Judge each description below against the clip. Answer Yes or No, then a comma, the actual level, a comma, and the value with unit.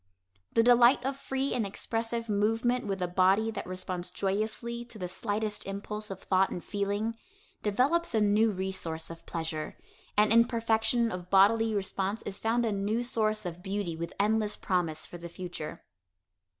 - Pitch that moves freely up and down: No, average, 3.2 semitones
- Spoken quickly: No, average, 165 wpm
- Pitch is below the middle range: No, high, 210 Hz